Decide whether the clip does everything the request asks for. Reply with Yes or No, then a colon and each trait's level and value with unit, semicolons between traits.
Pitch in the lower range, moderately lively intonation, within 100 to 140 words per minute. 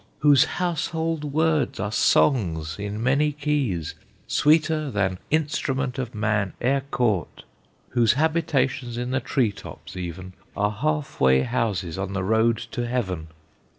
No: low, 120 Hz; wide, 6.9 semitones; slow, 135 wpm